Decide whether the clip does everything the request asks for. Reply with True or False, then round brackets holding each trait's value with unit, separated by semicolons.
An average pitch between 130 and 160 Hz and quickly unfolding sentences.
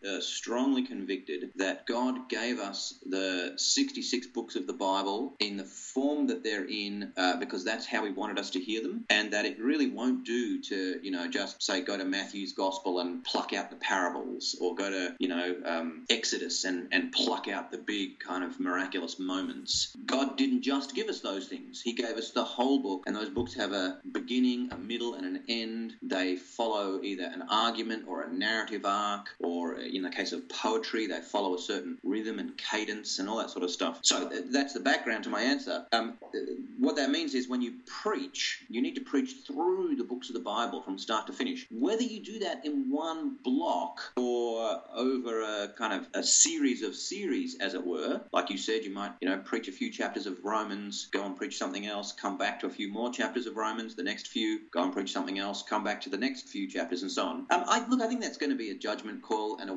True (140 Hz; 225 wpm)